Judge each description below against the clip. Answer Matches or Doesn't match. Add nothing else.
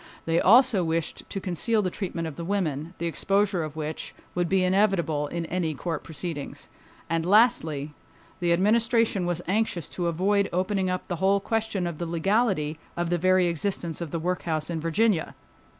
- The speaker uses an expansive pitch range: Doesn't match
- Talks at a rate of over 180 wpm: Doesn't match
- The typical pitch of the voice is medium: Matches